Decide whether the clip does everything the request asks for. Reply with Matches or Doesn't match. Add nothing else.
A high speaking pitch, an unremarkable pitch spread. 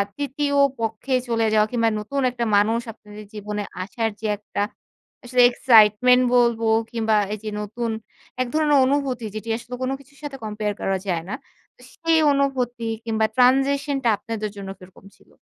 Matches